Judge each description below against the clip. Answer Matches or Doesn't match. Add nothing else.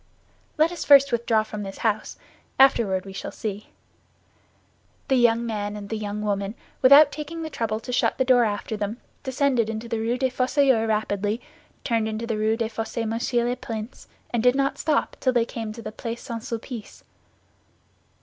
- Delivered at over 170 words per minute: Matches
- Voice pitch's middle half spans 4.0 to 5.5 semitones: Doesn't match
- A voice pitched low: Doesn't match